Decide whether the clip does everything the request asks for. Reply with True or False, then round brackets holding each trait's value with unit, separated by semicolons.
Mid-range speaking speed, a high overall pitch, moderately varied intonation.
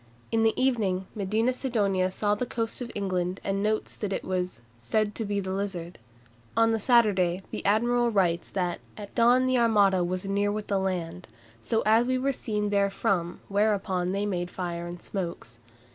True (180 wpm; 200 Hz; 3.3 semitones)